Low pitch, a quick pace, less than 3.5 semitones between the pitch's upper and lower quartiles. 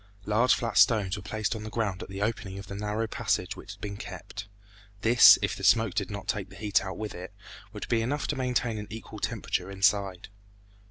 Yes: low, 105 Hz; fast, 220 wpm; narrow, 2.4 semitones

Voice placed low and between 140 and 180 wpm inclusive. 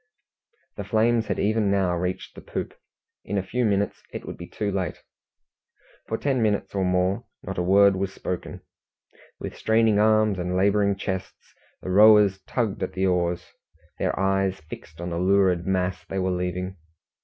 Yes: very low, 95 Hz; average, 170 wpm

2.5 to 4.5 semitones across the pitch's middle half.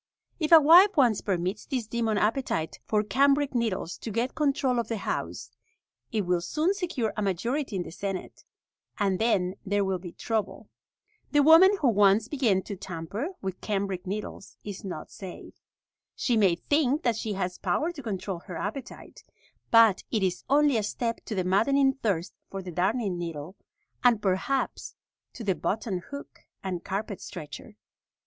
No: wide, 5.4 semitones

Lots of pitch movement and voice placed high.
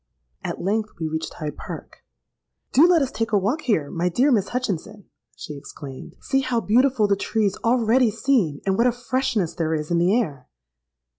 Yes: wide, 6.7 semitones; high, 215 Hz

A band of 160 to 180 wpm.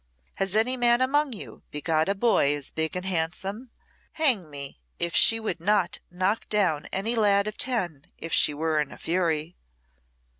Yes: average, 175 wpm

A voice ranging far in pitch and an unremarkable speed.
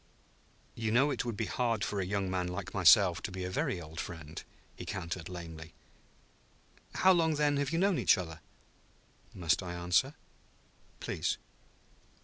Yes: wide, 5.8 semitones; average, 160 wpm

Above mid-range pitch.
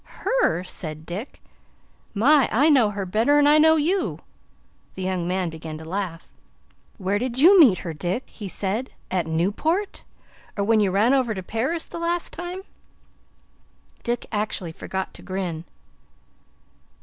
Yes: high, 210 Hz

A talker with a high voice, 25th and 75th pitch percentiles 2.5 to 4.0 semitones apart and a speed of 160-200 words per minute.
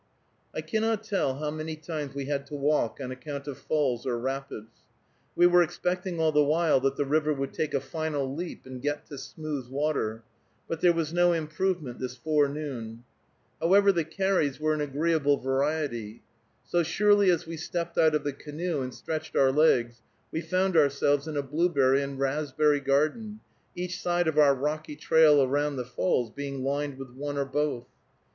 No: medium, 150 Hz; average, 3.0 semitones; average, 180 wpm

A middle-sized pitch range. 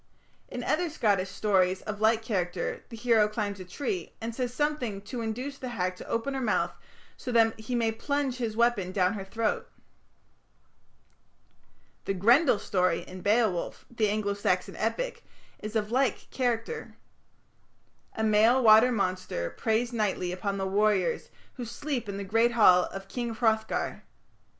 Yes: average, 3.4 semitones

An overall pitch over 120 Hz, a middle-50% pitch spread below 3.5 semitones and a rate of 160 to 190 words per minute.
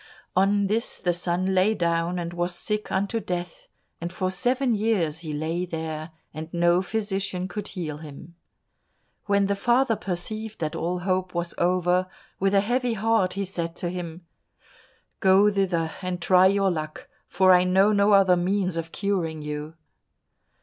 Yes: medium, 185 Hz; narrow, 2.6 semitones; average, 165 wpm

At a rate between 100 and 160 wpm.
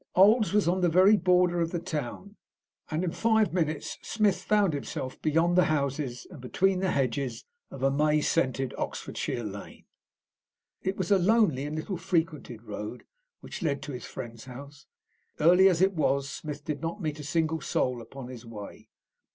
No: average, 175 wpm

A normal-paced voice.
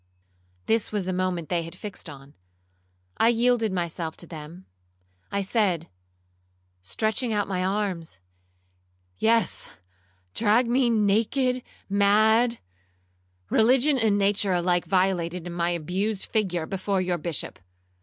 No: slow, 110 wpm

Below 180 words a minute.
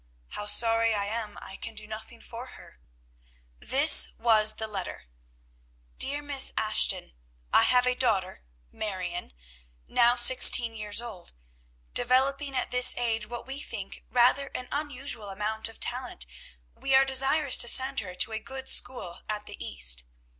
Yes: average, 155 wpm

